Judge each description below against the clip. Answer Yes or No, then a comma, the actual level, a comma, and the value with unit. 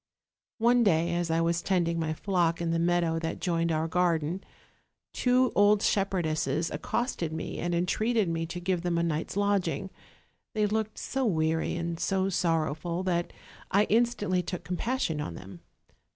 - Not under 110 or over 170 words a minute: Yes, average, 160 wpm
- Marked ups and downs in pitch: No, average, 3.4 semitones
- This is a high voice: No, medium, 175 Hz